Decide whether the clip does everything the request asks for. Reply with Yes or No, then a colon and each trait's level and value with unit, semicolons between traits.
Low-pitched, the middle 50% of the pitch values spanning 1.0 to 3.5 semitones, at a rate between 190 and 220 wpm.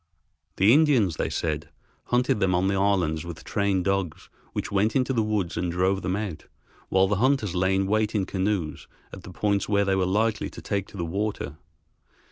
Yes: very low, 95 Hz; narrow, 2.5 semitones; average, 200 wpm